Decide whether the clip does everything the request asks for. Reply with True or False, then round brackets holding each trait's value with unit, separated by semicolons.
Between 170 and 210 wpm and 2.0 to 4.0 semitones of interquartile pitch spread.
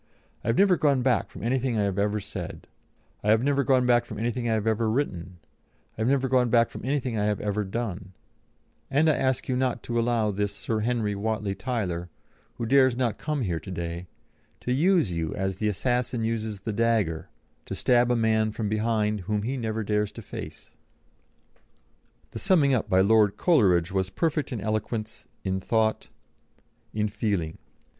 True (185 wpm; 3.4 semitones)